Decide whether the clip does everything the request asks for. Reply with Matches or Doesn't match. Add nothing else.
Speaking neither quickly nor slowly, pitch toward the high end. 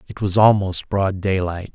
Doesn't match